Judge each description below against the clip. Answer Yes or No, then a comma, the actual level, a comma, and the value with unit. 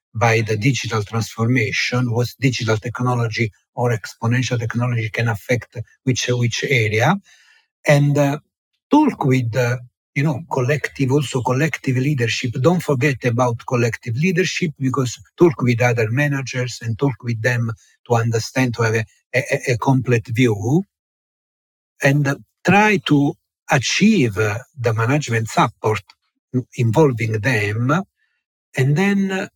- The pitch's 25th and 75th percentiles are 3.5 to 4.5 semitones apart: Yes, average, 3.8 semitones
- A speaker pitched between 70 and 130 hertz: Yes, low, 125 Hz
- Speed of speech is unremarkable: No, slow, 130 wpm